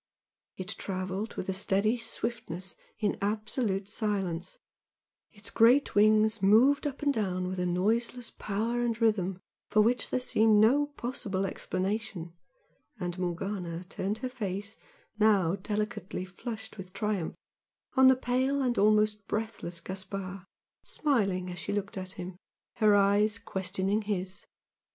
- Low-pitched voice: No, high, 205 Hz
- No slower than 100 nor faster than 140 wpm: Yes, slow, 135 wpm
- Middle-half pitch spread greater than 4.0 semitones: No, average, 3.1 semitones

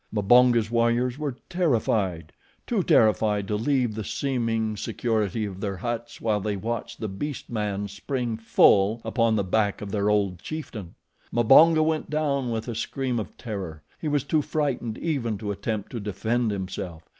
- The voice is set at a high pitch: No, low, 110 Hz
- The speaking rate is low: No, average, 165 wpm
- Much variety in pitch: No, average, 3.4 semitones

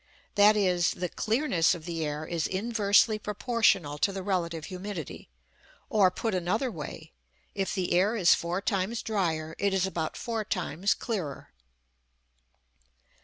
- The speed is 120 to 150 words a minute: Yes, average, 140 wpm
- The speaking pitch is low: No, high, 190 Hz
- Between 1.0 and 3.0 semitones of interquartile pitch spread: No, average, 3.8 semitones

